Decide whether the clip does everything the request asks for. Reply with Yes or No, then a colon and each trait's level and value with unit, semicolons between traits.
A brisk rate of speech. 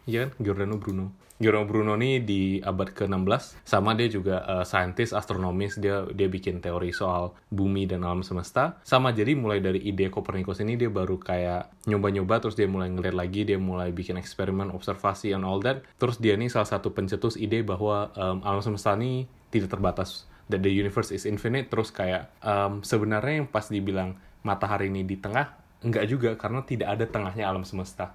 Yes: fast, 185 wpm